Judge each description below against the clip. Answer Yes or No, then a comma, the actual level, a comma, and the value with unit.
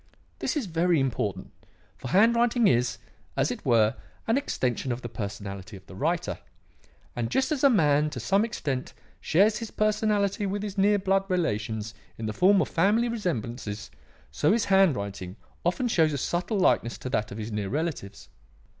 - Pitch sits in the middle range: Yes, medium, 165 Hz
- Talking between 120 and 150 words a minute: No, average, 170 wpm